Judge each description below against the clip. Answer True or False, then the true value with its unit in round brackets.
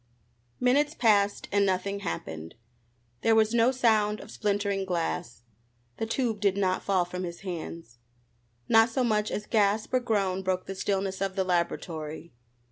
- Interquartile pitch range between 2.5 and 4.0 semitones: True (3.1 semitones)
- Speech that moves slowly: False (155 wpm)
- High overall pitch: True (200 Hz)